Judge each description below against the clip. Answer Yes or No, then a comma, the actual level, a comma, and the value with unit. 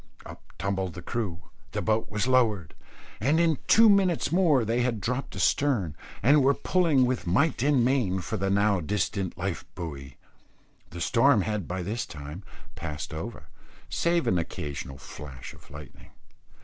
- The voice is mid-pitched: No, low, 105 Hz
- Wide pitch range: Yes, wide, 7.4 semitones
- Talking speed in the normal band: Yes, average, 160 wpm